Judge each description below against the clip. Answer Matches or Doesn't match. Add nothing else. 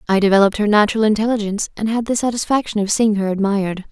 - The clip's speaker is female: Matches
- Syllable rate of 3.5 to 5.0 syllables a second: Doesn't match